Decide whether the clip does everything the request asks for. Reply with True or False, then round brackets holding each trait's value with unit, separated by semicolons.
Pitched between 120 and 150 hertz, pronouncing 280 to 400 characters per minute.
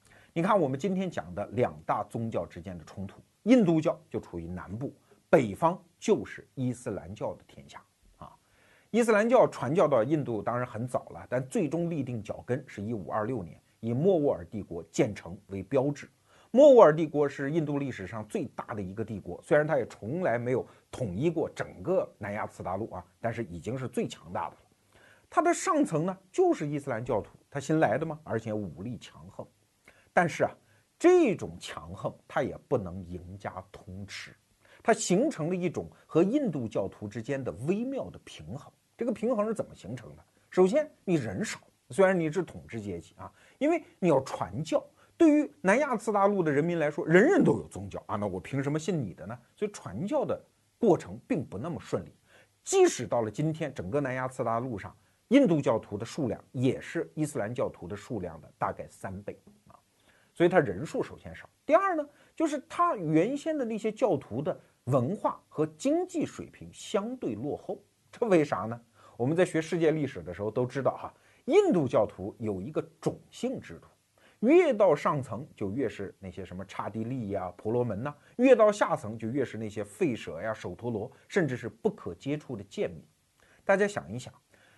True (140 Hz; 285 characters per minute)